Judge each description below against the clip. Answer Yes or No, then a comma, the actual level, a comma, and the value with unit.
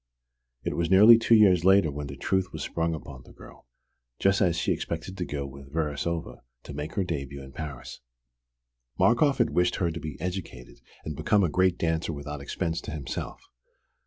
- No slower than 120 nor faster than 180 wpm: No, average, 190 wpm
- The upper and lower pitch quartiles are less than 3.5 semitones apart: No, average, 4.3 semitones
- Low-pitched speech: Yes, very low, 80 Hz